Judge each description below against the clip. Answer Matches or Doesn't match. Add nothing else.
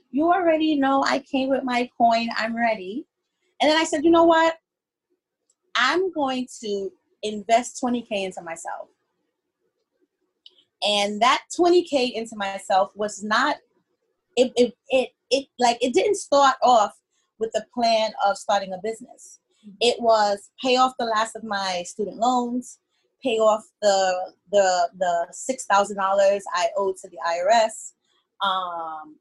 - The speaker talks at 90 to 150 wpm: Matches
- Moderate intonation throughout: Doesn't match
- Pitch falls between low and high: Doesn't match